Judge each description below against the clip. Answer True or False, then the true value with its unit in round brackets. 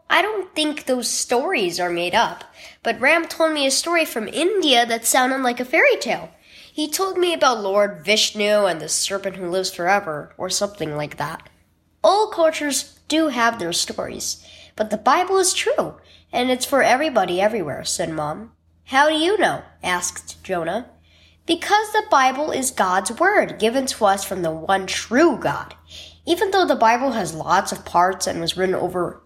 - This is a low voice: False (240 Hz)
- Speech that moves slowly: False (180 wpm)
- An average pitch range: False (8.9 semitones)